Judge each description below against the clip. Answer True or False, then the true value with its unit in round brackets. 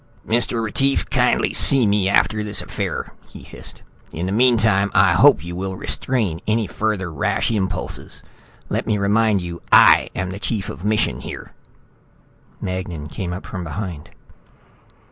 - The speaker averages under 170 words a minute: True (145 wpm)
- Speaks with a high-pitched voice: False (100 Hz)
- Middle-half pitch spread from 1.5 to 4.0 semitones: True (3.2 semitones)